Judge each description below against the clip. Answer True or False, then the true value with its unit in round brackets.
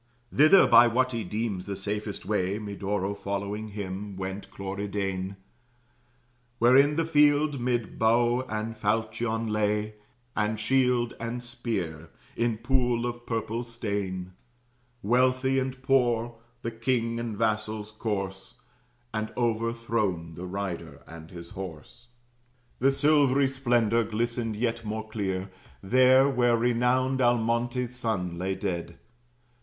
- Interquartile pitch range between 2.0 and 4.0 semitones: True (3.2 semitones)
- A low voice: True (115 Hz)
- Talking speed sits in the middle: False (120 wpm)